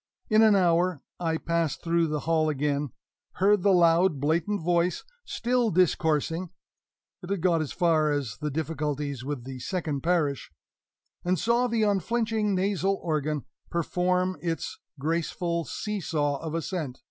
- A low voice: No, medium, 170 Hz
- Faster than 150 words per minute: No, average, 140 wpm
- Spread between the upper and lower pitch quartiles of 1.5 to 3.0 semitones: No, average, 3.5 semitones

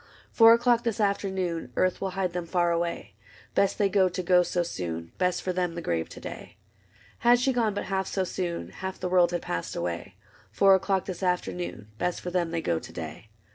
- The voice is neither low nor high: Yes, medium, 180 Hz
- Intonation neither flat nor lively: No, narrow, 2.3 semitones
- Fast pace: Yes, fast, 215 wpm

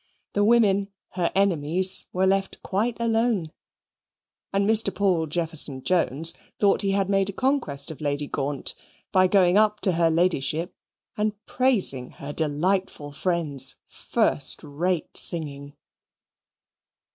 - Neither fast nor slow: No, slow, 125 wpm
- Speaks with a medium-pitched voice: Yes, medium, 180 Hz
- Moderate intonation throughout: Yes, average, 5.0 semitones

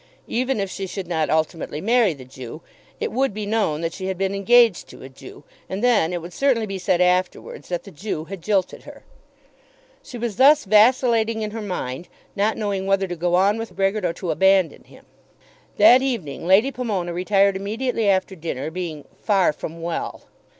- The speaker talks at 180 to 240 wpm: Yes, average, 190 wpm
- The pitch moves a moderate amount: Yes, average, 4.1 semitones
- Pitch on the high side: Yes, high, 195 Hz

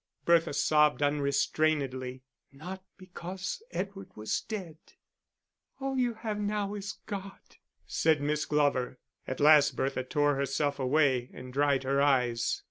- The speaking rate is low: Yes, slow, 125 wpm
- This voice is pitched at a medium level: Yes, medium, 150 Hz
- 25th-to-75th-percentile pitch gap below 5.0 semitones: No, wide, 5.6 semitones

